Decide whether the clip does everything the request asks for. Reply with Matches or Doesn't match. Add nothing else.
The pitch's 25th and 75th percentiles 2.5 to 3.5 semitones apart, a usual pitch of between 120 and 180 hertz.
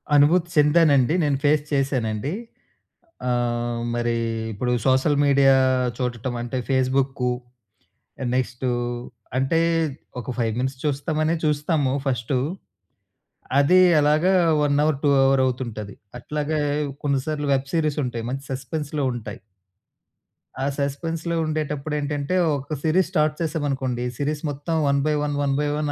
Matches